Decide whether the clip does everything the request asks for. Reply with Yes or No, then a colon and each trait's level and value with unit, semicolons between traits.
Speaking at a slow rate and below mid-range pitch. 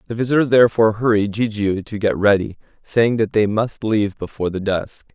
No: average, 185 wpm; low, 110 Hz